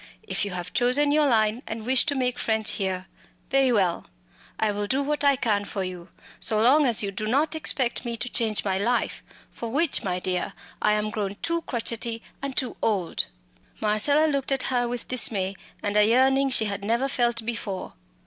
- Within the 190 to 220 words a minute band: Yes, average, 195 wpm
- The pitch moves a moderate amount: Yes, average, 4.4 semitones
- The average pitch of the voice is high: Yes, high, 230 Hz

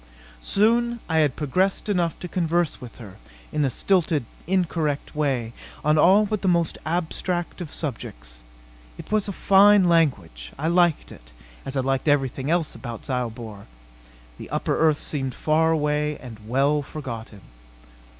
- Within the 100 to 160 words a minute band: Yes, average, 150 wpm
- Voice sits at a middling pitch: Yes, medium, 150 Hz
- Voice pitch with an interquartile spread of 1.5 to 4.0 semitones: No, average, 5.1 semitones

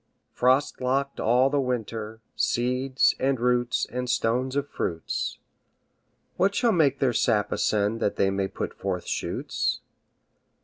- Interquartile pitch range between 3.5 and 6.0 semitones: No, average, 3.1 semitones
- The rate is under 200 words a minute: Yes, slow, 135 wpm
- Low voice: Yes, low, 125 Hz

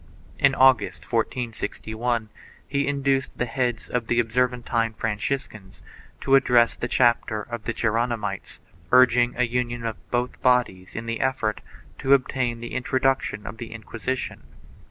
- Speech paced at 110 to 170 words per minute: Yes, average, 150 wpm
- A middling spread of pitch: No, narrow, 2.0 semitones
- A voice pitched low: Yes, low, 120 Hz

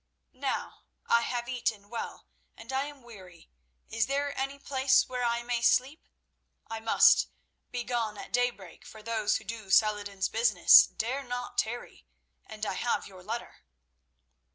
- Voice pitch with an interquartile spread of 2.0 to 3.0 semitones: Yes, narrow, 2.5 semitones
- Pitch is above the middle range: Yes, high, 235 Hz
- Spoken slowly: No, average, 155 wpm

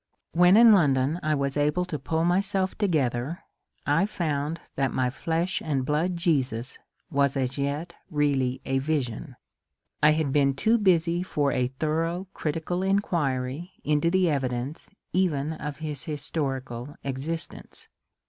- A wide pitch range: No, average, 3.9 semitones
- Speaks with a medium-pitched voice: Yes, medium, 150 Hz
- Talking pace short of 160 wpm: Yes, average, 140 wpm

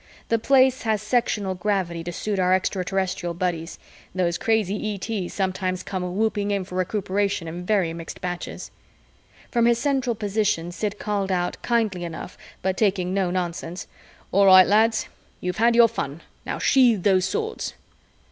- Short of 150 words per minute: No, average, 155 wpm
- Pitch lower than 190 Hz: No, high, 195 Hz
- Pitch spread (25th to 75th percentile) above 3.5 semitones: No, average, 3.2 semitones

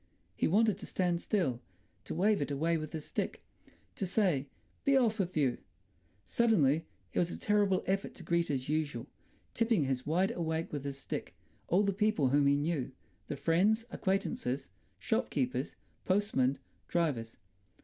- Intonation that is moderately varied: No, wide, 6.0 semitones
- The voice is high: No, medium, 165 Hz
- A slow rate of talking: No, average, 150 wpm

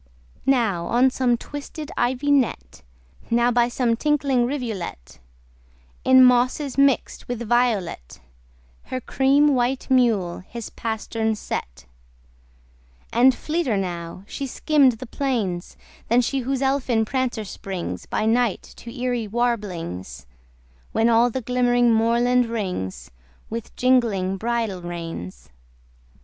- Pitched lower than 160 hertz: No, high, 235 Hz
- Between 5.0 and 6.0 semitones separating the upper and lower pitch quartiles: No, average, 4.2 semitones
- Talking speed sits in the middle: No, slow, 115 wpm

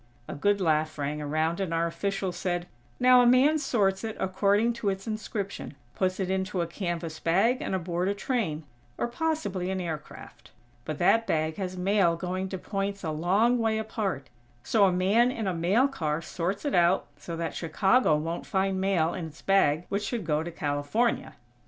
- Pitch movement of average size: Yes, average, 3.9 semitones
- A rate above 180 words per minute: Yes, average, 190 wpm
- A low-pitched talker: No, high, 190 Hz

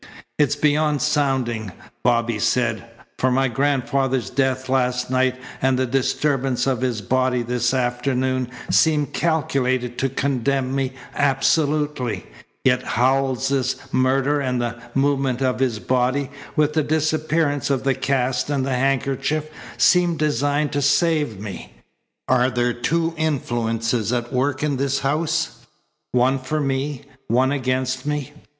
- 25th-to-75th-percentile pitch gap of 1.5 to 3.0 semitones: Yes, narrow, 2.4 semitones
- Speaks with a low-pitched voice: Yes, low, 130 Hz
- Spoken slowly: Yes, slow, 130 wpm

